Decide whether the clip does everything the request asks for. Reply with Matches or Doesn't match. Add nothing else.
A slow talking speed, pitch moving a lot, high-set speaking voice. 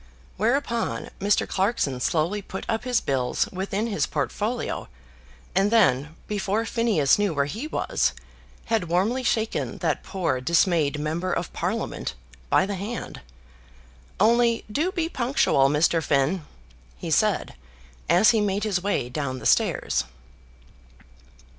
Matches